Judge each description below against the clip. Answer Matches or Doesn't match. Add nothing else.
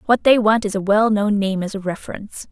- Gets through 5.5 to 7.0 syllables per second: Matches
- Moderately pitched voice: Doesn't match